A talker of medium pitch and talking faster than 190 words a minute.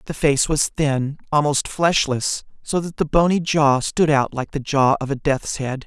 Yes: medium, 145 Hz; fast, 205 wpm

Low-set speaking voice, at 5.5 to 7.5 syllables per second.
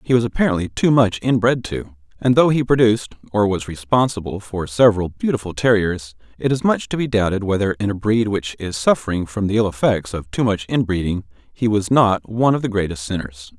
Yes: low, 105 Hz; 5.7 syllables/s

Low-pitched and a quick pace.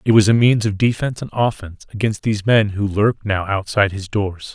Yes: low, 105 Hz; fast, 225 wpm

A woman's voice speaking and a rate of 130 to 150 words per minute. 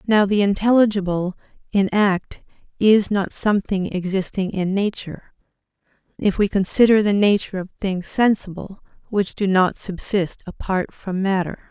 Yes: female; slow, 135 wpm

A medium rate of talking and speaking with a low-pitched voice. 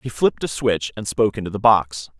No: fast, 245 wpm; low, 105 Hz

